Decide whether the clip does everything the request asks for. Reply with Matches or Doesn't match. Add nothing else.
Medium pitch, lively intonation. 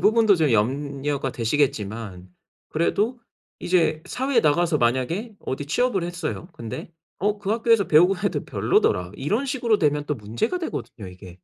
Matches